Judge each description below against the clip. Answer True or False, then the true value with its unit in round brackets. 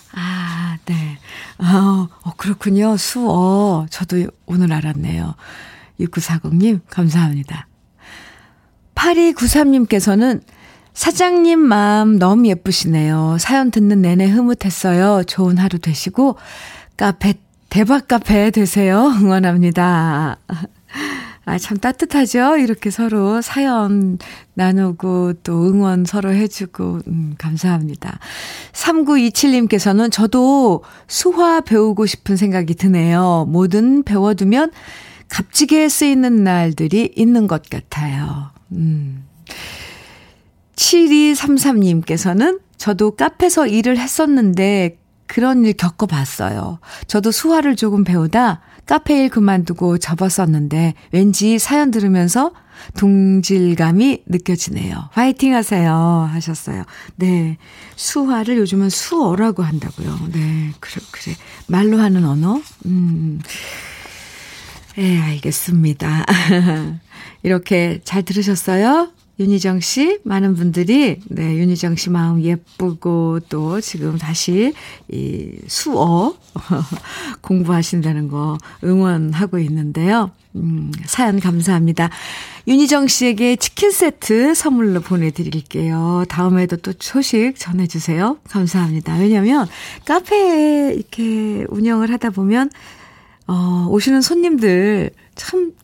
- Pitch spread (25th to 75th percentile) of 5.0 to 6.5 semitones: True (5.3 semitones)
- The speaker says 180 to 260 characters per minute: True (230 characters per minute)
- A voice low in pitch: False (190 Hz)